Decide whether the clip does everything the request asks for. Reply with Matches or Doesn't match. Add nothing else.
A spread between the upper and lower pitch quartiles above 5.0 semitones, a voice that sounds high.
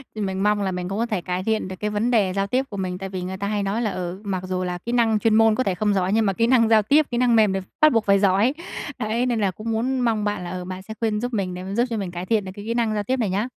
Doesn't match